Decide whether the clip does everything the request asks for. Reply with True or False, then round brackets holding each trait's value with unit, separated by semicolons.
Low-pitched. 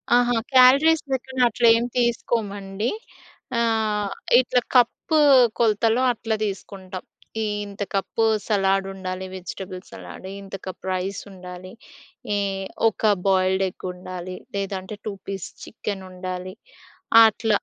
False (200 Hz)